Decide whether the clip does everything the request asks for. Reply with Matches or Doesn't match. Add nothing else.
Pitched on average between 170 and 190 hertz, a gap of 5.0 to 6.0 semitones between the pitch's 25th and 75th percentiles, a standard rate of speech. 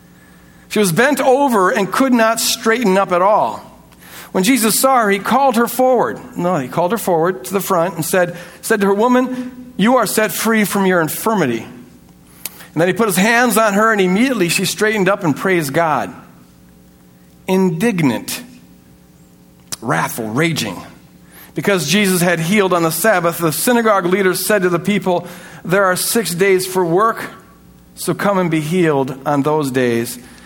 Matches